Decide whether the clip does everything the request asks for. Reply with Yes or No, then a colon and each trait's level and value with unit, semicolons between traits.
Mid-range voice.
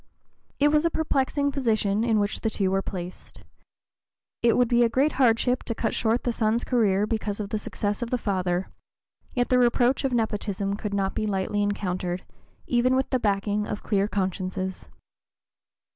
No: high, 215 Hz